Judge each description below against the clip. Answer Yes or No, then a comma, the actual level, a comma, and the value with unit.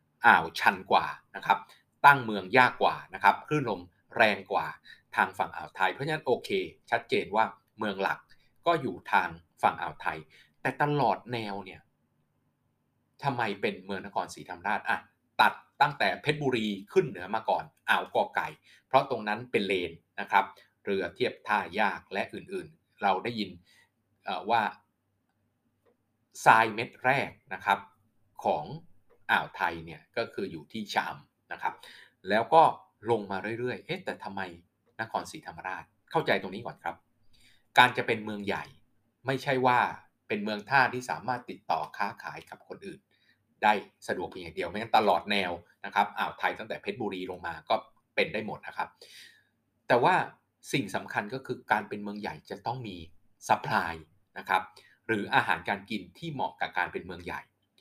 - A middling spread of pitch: Yes, average, 4.3 semitones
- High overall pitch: No, low, 105 Hz